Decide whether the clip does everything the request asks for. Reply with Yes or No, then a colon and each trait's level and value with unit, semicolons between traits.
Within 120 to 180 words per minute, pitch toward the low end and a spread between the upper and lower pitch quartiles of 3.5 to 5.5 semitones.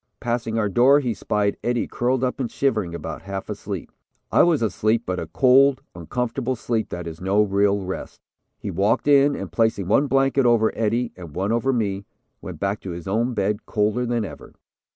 No: average, 195 wpm; low, 110 Hz; average, 4.0 semitones